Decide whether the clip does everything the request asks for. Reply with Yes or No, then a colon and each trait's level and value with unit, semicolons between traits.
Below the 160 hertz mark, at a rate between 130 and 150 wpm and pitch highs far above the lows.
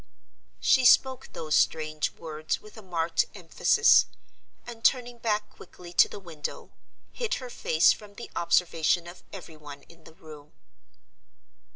No: medium, 175 Hz; average, 145 wpm; wide, 6.0 semitones